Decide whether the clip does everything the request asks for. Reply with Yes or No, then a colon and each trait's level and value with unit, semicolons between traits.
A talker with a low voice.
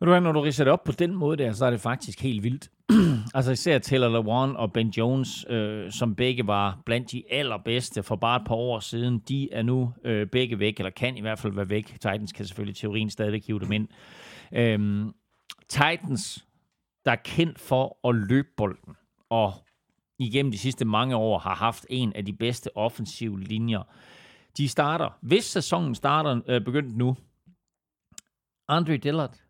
Yes: low, 120 Hz